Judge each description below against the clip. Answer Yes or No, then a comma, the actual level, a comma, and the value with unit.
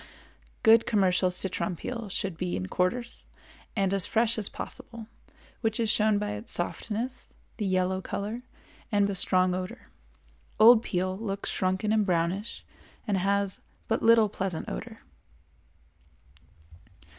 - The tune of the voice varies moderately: Yes, average, 3.1 semitones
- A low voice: No, high, 200 Hz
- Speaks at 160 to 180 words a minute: No, slow, 135 wpm